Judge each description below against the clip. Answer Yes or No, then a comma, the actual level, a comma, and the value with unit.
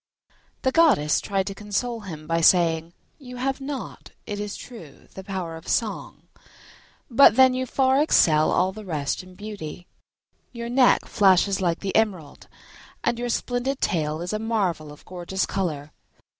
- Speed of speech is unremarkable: Yes, average, 160 wpm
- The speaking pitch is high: Yes, high, 195 Hz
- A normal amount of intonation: No, wide, 6.2 semitones